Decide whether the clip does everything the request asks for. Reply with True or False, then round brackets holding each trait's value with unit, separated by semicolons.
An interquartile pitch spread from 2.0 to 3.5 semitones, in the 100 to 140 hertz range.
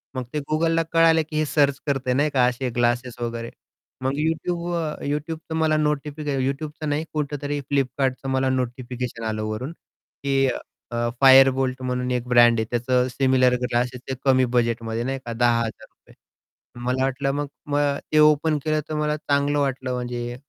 True (3.2 semitones; 135 Hz)